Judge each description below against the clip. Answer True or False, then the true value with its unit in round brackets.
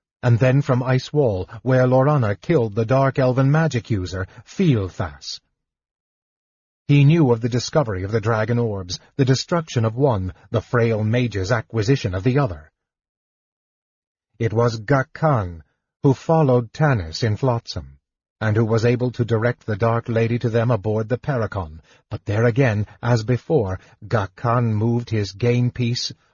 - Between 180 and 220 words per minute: False (150 wpm)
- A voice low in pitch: True (120 Hz)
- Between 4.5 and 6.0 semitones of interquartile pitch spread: False (3.3 semitones)